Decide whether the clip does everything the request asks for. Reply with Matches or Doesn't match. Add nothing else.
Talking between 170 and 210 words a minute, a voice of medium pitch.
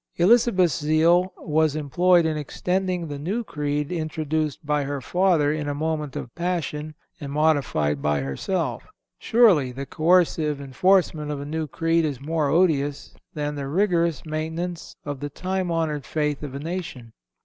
Doesn't match